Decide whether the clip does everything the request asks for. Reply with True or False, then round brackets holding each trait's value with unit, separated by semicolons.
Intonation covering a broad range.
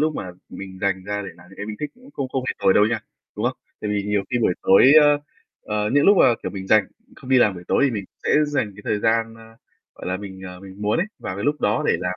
False (4.7 semitones)